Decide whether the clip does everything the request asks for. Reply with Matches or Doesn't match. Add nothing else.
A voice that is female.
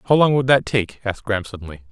Doesn't match